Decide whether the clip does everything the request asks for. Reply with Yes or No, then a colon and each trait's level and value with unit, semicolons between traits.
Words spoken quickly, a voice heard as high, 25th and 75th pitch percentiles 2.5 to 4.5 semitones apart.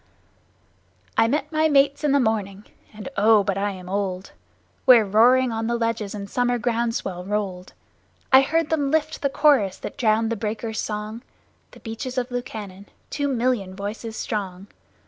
No: average, 165 wpm; high, 225 Hz; average, 3.9 semitones